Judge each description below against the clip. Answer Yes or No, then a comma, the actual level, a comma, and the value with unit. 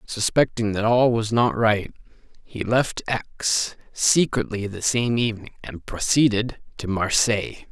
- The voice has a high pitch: No, low, 110 Hz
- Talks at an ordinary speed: No, slow, 130 wpm